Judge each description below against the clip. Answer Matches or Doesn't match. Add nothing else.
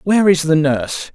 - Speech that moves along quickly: Matches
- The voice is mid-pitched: Matches